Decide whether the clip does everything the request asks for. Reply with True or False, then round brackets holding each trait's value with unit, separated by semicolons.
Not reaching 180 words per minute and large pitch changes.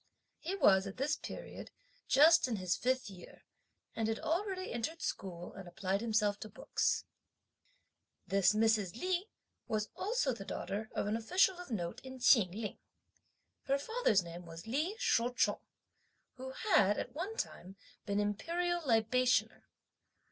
True (150 wpm; 8.3 semitones)